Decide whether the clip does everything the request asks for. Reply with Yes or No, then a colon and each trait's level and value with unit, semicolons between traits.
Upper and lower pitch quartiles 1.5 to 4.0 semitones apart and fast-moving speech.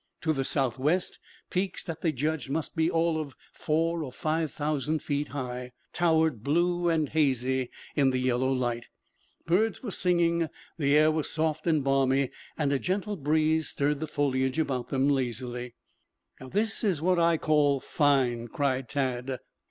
No: average, 3.6 semitones; average, 160 wpm